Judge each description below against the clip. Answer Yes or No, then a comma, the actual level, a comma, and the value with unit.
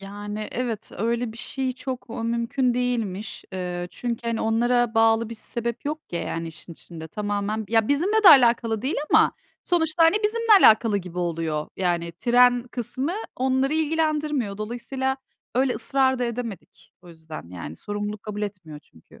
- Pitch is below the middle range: No, high, 230 Hz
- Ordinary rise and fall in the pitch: Yes, average, 4.4 semitones